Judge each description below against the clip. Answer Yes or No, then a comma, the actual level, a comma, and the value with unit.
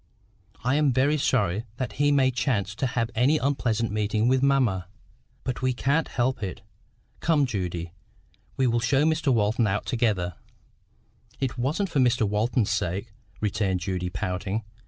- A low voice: Yes, low, 120 Hz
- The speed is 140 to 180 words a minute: Yes, average, 155 wpm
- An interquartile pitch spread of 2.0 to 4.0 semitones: No, average, 4.5 semitones